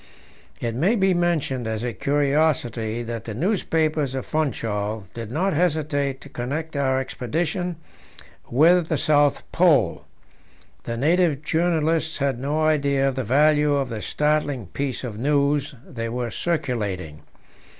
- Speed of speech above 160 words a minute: No, average, 140 wpm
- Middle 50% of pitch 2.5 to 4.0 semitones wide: No, average, 4.4 semitones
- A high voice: No, medium, 140 Hz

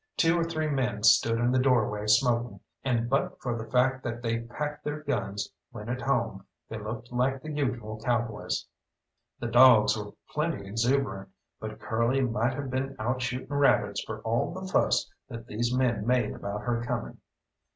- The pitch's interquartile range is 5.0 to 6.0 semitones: No, average, 2.8 semitones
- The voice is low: Yes, low, 120 Hz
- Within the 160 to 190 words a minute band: Yes, average, 175 wpm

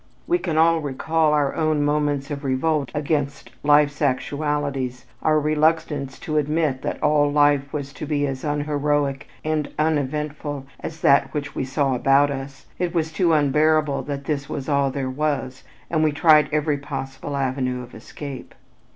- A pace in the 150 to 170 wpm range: Yes, average, 160 wpm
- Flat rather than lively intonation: Yes, narrow, 1.7 semitones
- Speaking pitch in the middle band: Yes, medium, 145 Hz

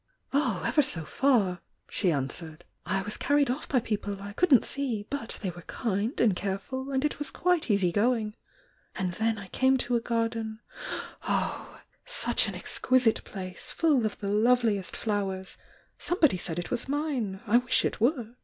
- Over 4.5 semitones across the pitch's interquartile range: Yes, average, 5.1 semitones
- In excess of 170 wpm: Yes, average, 180 wpm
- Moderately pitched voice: No, high, 225 Hz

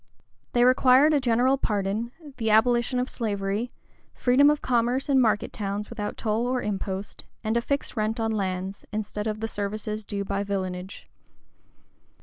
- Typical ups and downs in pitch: Yes, average, 3.5 semitones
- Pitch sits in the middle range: No, high, 220 Hz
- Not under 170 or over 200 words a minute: No, average, 155 wpm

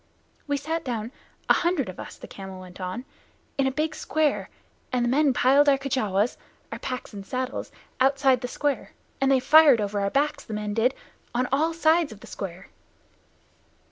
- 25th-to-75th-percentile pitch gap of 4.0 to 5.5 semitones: Yes, average, 5.2 semitones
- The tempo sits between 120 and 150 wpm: No, average, 175 wpm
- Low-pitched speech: No, very high, 260 Hz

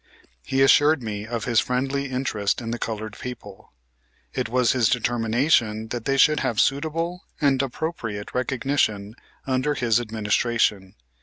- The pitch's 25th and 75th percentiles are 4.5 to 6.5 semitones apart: No, average, 3.8 semitones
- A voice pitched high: No, low, 120 Hz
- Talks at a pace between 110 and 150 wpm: Yes, average, 140 wpm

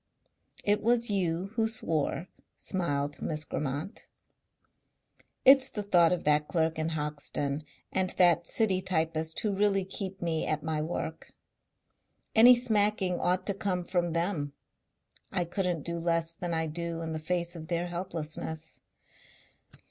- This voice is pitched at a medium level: Yes, medium, 170 Hz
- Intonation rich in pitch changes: No, average, 3.2 semitones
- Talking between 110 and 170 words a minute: Yes, average, 140 wpm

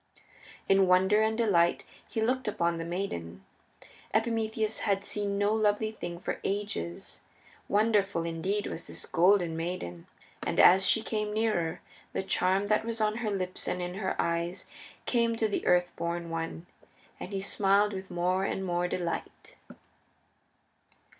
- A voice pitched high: Yes, high, 195 Hz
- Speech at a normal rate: Yes, average, 150 wpm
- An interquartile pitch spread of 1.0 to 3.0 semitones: No, average, 3.5 semitones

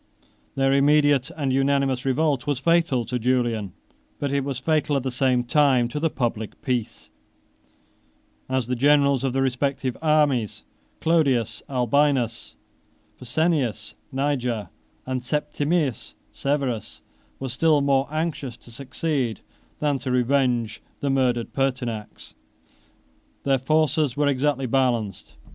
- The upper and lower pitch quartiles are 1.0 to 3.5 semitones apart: Yes, average, 2.7 semitones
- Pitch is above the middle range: No, low, 135 Hz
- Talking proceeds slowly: Yes, slow, 120 wpm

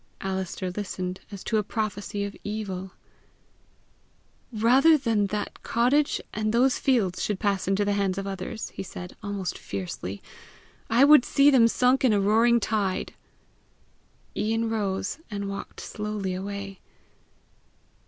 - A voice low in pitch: No, high, 205 Hz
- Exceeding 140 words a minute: No, slow, 135 wpm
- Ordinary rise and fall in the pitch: Yes, average, 3.0 semitones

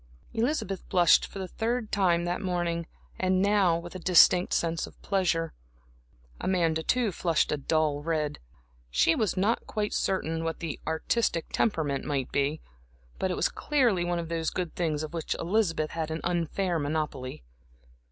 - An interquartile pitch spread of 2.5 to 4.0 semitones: Yes, average, 2.9 semitones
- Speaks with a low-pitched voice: No, medium, 170 Hz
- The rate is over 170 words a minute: No, average, 160 wpm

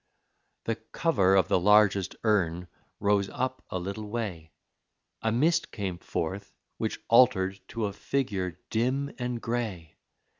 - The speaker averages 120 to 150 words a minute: Yes, slow, 135 wpm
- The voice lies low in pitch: Yes, low, 105 Hz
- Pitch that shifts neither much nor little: Yes, average, 4.2 semitones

